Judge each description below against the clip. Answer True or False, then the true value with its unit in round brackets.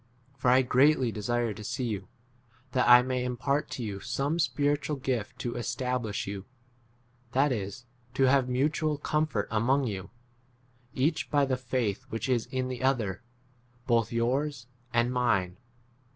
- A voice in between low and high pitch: False (125 Hz)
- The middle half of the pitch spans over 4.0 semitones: False (2.8 semitones)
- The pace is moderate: True (155 wpm)